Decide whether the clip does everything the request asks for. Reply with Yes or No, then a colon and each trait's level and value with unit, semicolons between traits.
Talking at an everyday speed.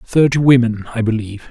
Yes: average, 160 wpm